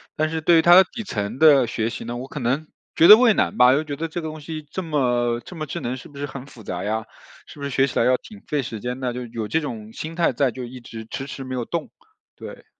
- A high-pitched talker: No, low, 135 Hz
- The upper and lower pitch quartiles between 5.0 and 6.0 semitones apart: No, average, 4.6 semitones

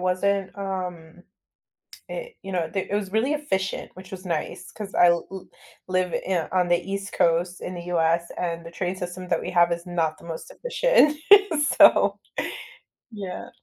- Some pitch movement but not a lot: No, narrow, 2.1 semitones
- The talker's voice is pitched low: No, medium, 180 Hz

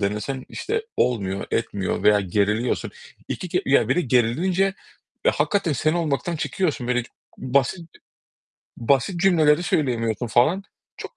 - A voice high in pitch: No, low, 135 Hz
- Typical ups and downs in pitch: No, wide, 7.0 semitones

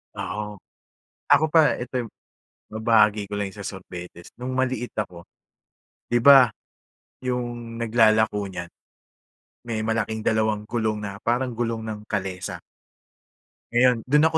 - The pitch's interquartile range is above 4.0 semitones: No, average, 2.8 semitones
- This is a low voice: Yes, low, 110 Hz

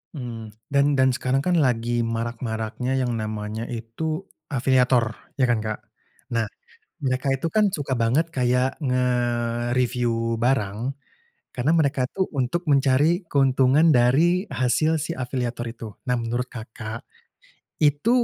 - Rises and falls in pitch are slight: Yes, narrow, 2.3 semitones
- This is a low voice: Yes, low, 125 Hz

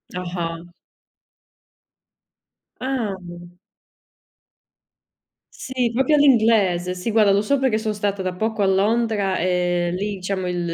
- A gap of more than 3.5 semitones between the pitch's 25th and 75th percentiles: Yes, average, 3.9 semitones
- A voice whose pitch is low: No, high, 200 Hz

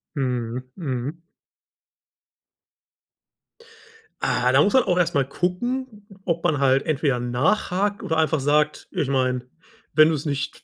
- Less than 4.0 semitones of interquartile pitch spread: No, average, 5.3 semitones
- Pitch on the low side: No, medium, 150 Hz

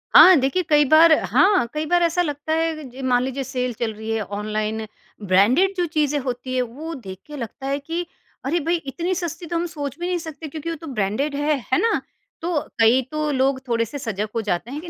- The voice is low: No, very high, 285 Hz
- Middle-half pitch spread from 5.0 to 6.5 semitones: Yes, average, 5.3 semitones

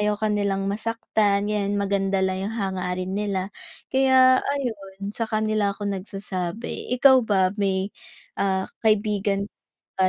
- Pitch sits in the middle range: No, high, 200 Hz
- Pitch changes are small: Yes, narrow, 1.9 semitones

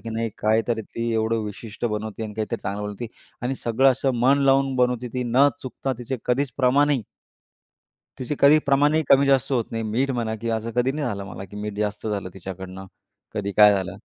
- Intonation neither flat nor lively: Yes, average, 4.0 semitones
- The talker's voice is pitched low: Yes, low, 115 Hz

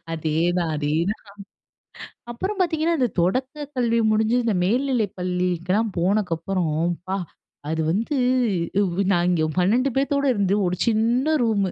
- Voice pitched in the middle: No, high, 205 Hz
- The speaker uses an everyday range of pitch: No, wide, 6.0 semitones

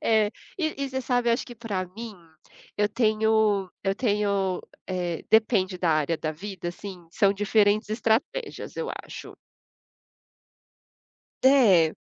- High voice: Yes, high, 210 Hz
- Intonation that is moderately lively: Yes, average, 3.4 semitones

